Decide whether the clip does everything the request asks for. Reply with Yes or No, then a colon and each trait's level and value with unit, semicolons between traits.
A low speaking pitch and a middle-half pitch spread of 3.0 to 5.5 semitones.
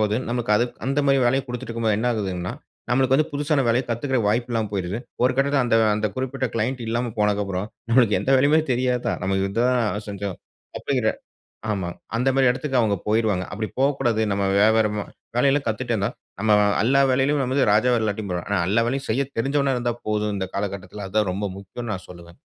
Yes: low, 115 Hz; average, 4.1 semitones